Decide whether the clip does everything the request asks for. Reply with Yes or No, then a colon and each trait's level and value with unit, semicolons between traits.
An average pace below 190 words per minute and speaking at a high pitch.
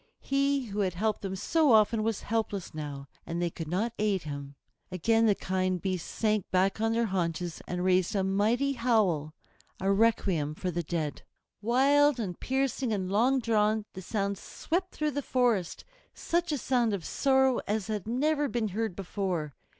Yes: average, 175 wpm; high, 210 Hz